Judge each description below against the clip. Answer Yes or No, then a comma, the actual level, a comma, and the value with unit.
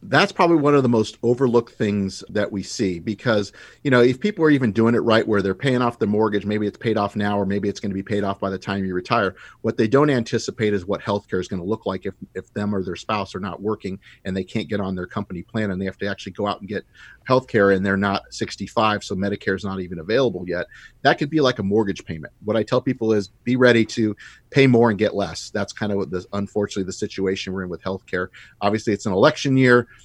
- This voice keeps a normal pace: No, fast, 265 wpm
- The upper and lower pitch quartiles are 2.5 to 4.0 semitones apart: Yes, average, 3.1 semitones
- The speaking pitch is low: Yes, low, 105 Hz